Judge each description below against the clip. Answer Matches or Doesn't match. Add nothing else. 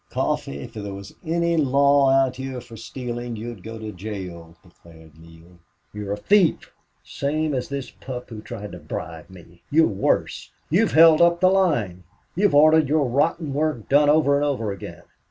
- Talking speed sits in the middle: Matches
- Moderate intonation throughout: Doesn't match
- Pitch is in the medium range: Doesn't match